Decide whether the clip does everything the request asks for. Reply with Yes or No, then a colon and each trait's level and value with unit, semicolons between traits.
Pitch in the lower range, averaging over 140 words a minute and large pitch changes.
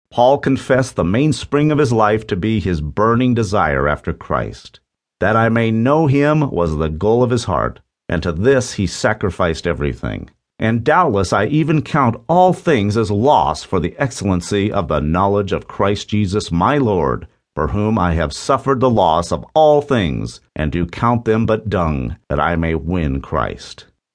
Yes: low, 105 Hz; average, 180 wpm; wide, 6.5 semitones